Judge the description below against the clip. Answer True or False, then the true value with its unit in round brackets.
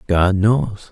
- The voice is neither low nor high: False (100 Hz)